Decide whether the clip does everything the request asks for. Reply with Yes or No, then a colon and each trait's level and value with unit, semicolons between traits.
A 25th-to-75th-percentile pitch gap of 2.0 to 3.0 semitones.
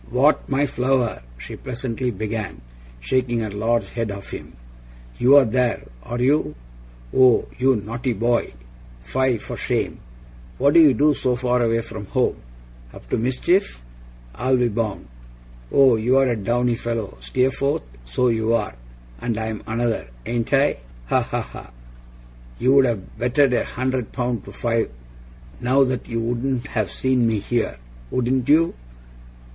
Yes: narrow, 2.6 semitones